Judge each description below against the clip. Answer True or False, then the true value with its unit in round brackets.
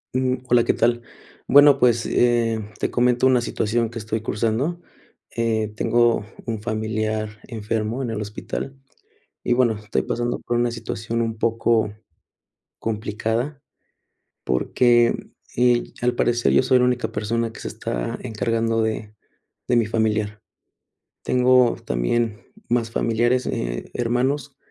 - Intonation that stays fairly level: True (1.9 semitones)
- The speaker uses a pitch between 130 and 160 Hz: False (115 Hz)